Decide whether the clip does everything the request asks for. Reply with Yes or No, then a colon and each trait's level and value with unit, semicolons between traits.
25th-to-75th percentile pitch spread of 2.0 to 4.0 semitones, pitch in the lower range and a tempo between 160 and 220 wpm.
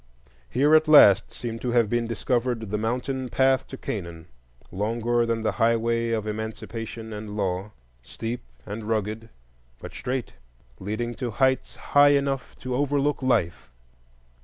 No: average, 3.1 semitones; low, 115 Hz; average, 140 wpm